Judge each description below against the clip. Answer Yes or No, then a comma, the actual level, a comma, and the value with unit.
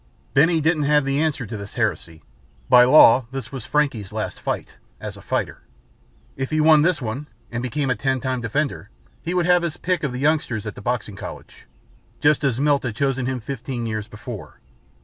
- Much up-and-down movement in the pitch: No, average, 4.0 semitones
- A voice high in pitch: No, low, 135 Hz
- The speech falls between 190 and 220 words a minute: Yes, average, 200 wpm